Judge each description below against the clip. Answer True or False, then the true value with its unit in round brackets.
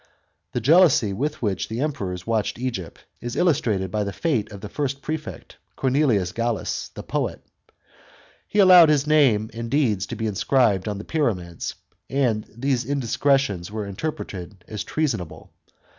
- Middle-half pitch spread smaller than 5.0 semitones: False (5.6 semitones)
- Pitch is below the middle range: True (115 Hz)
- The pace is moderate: True (155 wpm)